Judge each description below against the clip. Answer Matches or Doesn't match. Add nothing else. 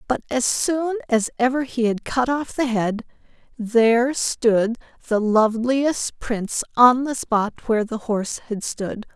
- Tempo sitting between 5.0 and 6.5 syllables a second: Doesn't match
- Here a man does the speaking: Doesn't match